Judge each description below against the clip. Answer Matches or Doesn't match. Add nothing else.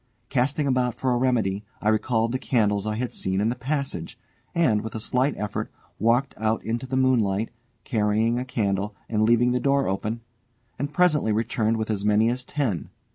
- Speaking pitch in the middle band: Doesn't match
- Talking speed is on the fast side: Doesn't match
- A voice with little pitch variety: Doesn't match